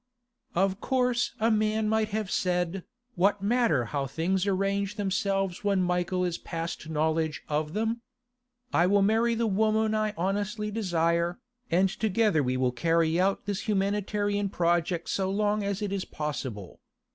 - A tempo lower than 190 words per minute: Yes, average, 150 wpm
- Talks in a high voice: Yes, high, 195 Hz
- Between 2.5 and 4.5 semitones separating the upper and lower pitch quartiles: Yes, average, 3.8 semitones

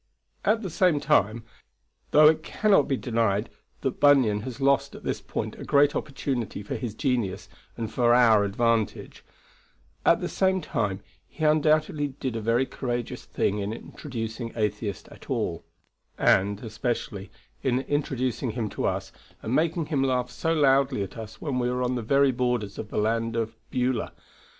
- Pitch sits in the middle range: No, low, 125 Hz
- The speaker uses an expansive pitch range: No, average, 4.0 semitones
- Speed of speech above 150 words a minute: Yes, average, 170 wpm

